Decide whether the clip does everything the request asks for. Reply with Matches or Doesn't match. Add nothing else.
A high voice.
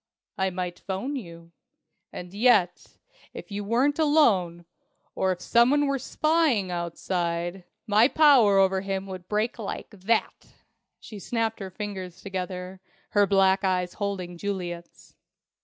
Matches